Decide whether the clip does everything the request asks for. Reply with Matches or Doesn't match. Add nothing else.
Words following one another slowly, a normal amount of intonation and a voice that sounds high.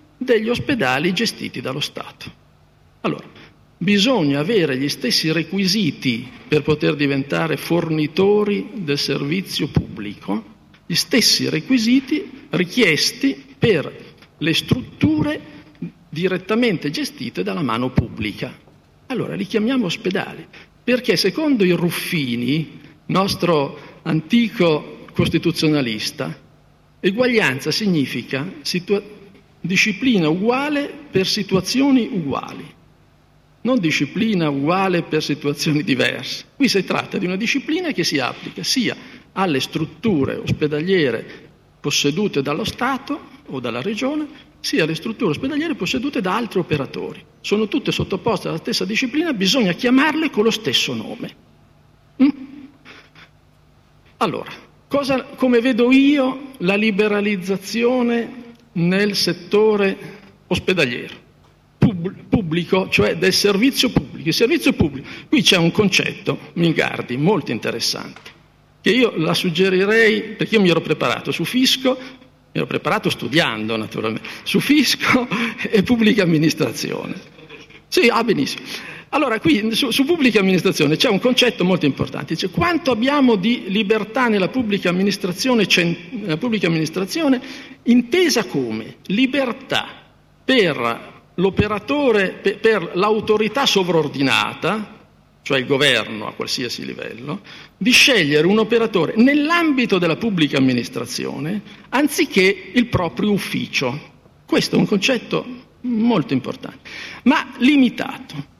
Doesn't match